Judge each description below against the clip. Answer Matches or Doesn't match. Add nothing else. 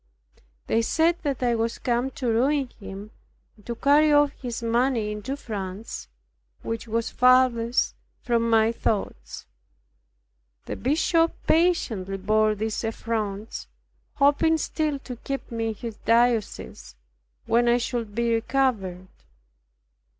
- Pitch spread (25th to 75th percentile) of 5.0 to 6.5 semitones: Doesn't match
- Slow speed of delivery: Matches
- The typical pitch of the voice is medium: Doesn't match